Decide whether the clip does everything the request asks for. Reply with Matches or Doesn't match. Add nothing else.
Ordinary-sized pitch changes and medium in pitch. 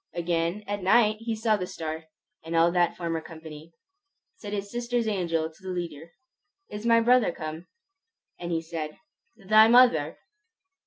Matches